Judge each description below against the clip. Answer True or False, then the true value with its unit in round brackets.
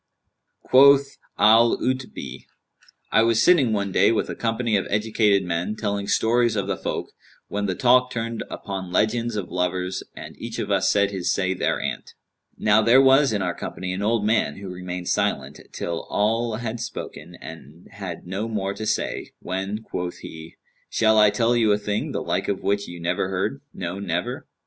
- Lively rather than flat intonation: False (3.6 semitones)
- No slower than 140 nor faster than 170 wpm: False (180 wpm)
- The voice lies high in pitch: False (105 Hz)